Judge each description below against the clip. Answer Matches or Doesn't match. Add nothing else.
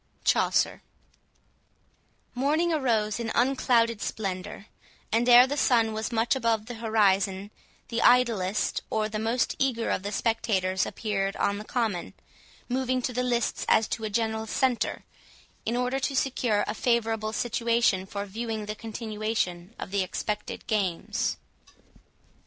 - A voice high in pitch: Matches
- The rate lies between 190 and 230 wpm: Doesn't match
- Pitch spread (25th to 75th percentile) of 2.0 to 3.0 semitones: Matches